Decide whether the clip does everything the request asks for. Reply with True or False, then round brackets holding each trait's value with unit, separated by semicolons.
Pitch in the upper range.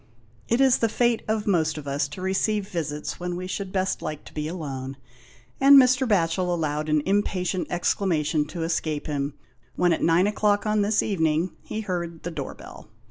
False (175 Hz)